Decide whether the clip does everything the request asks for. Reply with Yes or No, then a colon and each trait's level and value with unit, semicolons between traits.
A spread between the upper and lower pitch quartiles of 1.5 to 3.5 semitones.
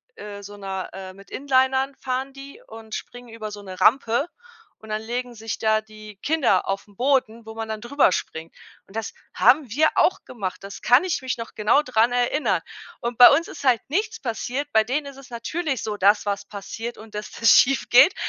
No: average, 4.0 semitones